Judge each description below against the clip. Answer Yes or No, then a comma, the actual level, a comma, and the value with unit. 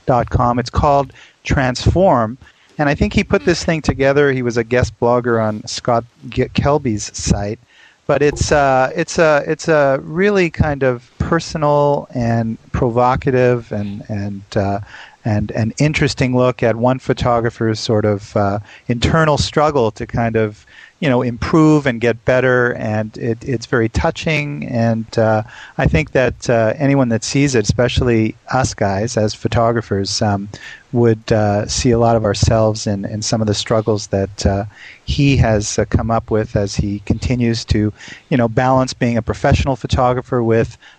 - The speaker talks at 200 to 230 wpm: No, average, 170 wpm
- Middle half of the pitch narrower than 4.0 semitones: Yes, average, 3.3 semitones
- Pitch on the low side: Yes, low, 120 Hz